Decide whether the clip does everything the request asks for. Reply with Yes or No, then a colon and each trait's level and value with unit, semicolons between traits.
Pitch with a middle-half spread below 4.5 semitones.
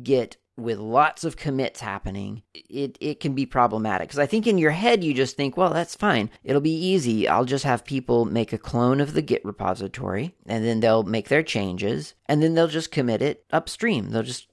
No: average, 5.1 semitones